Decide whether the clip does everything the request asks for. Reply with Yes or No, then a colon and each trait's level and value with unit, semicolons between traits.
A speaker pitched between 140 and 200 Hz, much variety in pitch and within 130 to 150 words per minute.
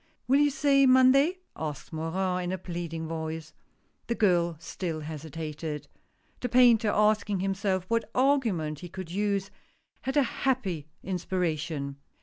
Yes: medium, 185 Hz; wide, 6.2 semitones; average, 140 wpm